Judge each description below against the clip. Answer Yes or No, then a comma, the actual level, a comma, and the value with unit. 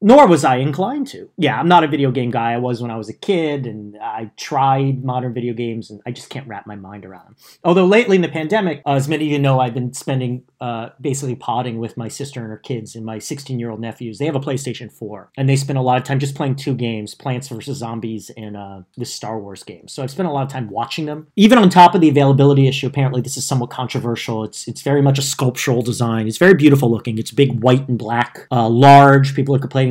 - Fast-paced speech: Yes, fast, 255 wpm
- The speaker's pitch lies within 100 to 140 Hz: Yes, low, 130 Hz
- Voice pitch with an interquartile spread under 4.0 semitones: Yes, average, 3.4 semitones